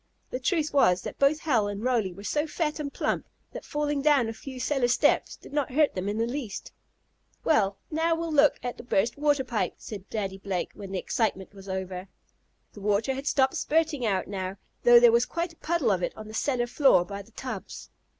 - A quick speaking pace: Yes, fast, 220 wpm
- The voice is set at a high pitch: Yes, high, 240 Hz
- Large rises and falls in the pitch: Yes, wide, 6.5 semitones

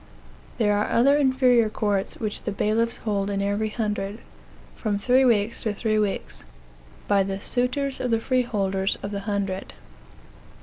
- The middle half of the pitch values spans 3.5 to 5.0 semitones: No, average, 3.0 semitones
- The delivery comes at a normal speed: Yes, average, 150 wpm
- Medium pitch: No, high, 215 Hz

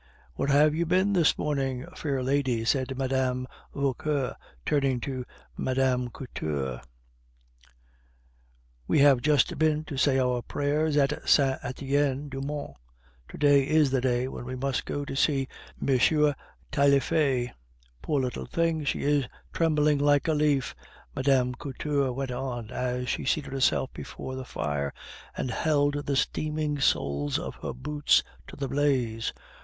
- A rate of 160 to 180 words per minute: No, average, 145 wpm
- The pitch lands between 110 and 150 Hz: Yes, low, 135 Hz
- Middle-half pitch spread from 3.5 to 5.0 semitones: No, narrow, 2.4 semitones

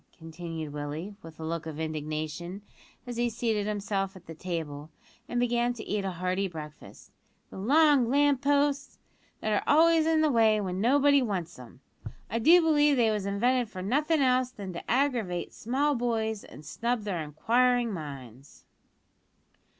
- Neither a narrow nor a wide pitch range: No, wide, 7.0 semitones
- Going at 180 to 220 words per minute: No, average, 165 wpm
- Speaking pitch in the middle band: No, high, 215 Hz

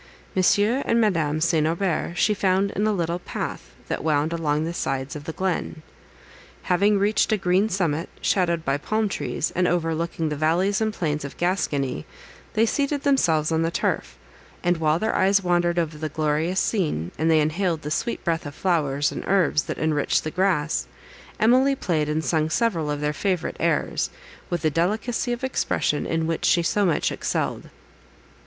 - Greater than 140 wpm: Yes, average, 180 wpm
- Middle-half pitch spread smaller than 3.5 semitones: No, average, 4.2 semitones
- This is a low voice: No, medium, 170 Hz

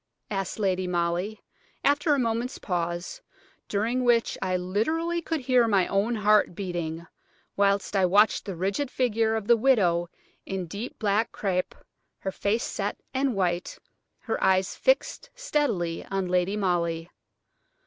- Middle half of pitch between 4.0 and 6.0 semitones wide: Yes, average, 4.7 semitones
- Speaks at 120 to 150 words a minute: Yes, average, 140 wpm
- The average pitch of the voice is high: Yes, high, 200 Hz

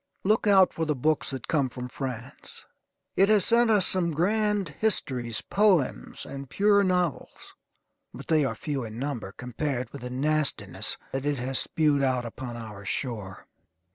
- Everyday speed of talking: Yes, average, 165 wpm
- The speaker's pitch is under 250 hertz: Yes, medium, 140 Hz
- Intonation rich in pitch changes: Yes, wide, 6.5 semitones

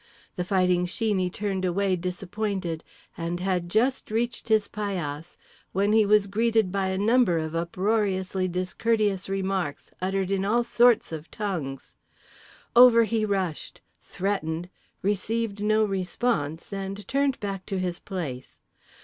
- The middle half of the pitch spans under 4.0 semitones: Yes, average, 3.0 semitones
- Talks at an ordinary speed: No, slow, 130 wpm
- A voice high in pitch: Yes, high, 195 Hz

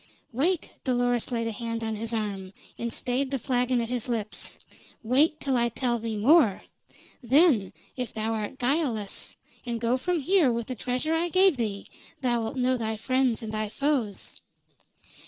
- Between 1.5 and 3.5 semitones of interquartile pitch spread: Yes, average, 3.1 semitones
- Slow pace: No, average, 170 wpm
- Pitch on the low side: No, high, 245 Hz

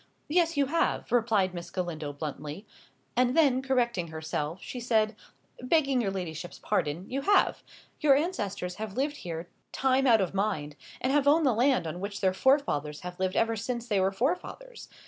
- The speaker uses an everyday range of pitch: No, wide, 7.0 semitones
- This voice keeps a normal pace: Yes, average, 175 wpm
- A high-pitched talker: Yes, high, 220 Hz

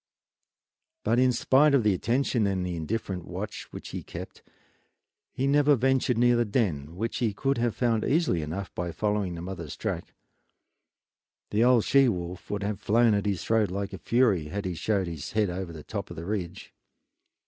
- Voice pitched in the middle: No, low, 105 Hz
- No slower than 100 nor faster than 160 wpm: No, average, 185 wpm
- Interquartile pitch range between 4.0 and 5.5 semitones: Yes, average, 5.0 semitones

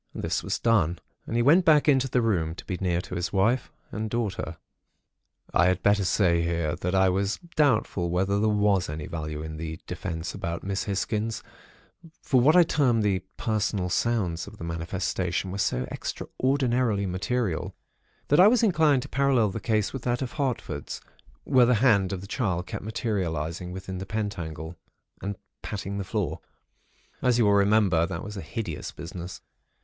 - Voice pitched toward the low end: Yes, low, 100 Hz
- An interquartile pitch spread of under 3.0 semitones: No, average, 5.1 semitones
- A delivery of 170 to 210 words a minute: Yes, average, 175 wpm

